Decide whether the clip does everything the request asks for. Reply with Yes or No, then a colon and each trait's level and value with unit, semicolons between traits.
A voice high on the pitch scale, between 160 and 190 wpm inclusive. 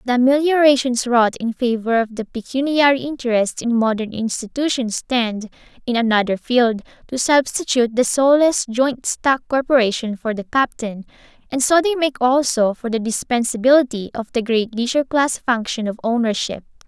No: high, 245 Hz; average, 150 wpm